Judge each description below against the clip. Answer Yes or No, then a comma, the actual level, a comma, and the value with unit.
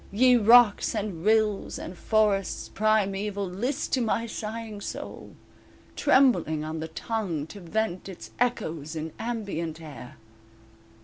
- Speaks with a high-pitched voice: Yes, high, 205 Hz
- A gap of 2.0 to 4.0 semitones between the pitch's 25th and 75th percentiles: No, average, 5.1 semitones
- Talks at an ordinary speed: No, slow, 125 wpm